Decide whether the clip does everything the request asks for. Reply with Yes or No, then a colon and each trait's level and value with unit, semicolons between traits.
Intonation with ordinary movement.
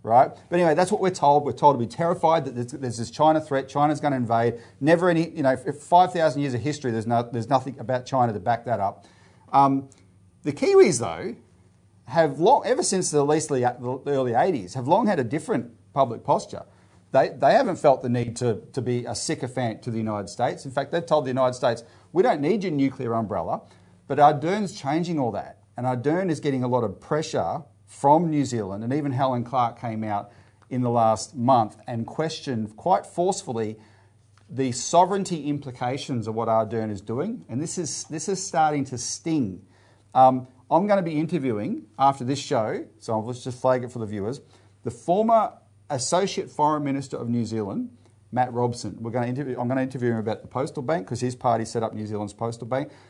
Yes: average, 4.5 semitones